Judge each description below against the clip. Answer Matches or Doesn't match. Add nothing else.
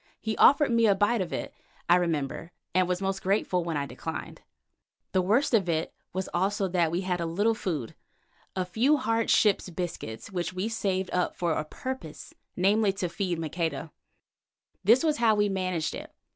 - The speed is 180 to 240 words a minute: Matches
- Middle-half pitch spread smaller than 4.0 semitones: Matches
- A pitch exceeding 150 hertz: Matches